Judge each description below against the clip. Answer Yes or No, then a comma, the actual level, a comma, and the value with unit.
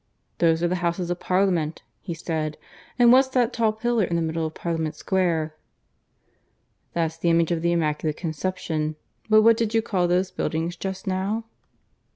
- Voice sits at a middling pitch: Yes, medium, 175 Hz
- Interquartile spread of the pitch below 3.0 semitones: No, average, 3.4 semitones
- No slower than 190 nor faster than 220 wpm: No, average, 175 wpm